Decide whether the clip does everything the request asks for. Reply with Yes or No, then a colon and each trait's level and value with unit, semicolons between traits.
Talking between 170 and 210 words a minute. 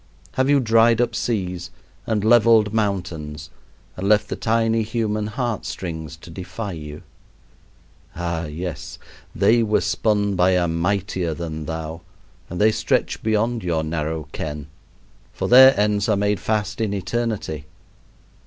No: average, 140 wpm